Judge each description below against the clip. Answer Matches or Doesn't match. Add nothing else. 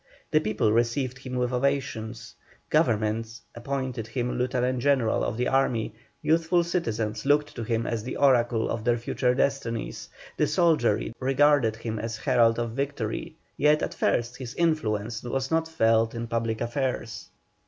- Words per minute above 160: Doesn't match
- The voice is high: Doesn't match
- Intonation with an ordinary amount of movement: Matches